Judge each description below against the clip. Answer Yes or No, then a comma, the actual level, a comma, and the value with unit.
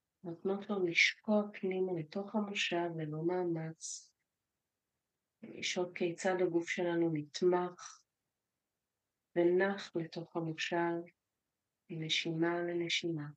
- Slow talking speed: Yes, slow, 80 wpm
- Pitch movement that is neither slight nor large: No, narrow, 1.8 semitones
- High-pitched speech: No, medium, 175 Hz